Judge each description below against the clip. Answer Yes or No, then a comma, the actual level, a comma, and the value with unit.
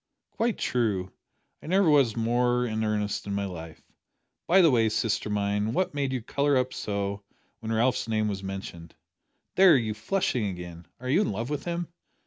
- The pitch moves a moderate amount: Yes, average, 4.9 semitones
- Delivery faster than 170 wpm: Yes, average, 180 wpm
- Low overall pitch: Yes, low, 115 Hz